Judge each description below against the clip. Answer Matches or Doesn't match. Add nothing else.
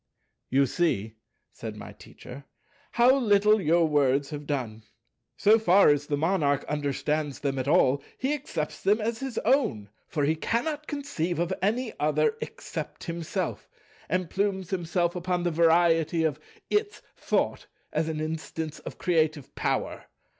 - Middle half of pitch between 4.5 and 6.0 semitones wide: Matches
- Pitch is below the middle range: Doesn't match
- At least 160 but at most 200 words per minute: Doesn't match